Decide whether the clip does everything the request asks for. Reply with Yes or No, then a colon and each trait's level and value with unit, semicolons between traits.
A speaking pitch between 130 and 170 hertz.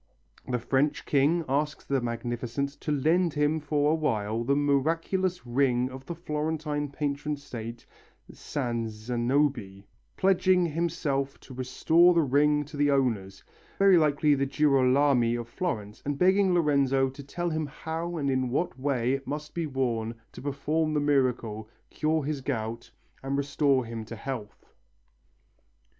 Yes: medium, 140 Hz